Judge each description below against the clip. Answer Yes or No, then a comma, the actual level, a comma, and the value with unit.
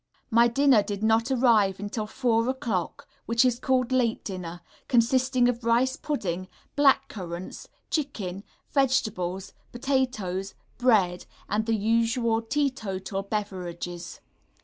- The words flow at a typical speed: No, slow, 120 wpm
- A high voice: Yes, high, 225 Hz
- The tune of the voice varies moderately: Yes, average, 4.6 semitones